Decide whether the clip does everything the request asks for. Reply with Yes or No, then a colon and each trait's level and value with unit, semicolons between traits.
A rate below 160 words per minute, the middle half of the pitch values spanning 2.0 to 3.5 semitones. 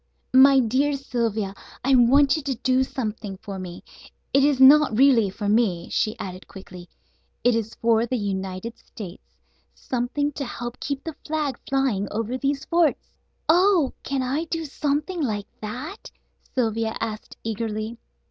No: average, 150 wpm; average, 4.5 semitones